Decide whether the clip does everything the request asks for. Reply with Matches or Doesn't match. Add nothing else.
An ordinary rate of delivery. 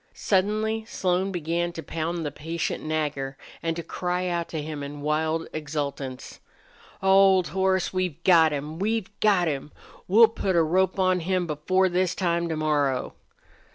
Matches